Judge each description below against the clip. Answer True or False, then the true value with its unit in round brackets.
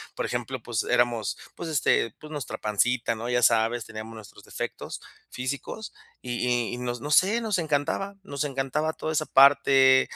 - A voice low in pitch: True (130 Hz)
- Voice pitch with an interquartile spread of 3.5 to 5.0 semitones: True (4.2 semitones)